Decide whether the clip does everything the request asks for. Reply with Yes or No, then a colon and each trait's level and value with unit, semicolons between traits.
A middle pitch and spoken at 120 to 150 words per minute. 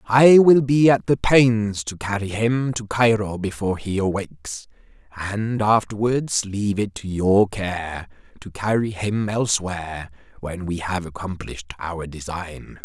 No: low, 100 Hz; average, 145 wpm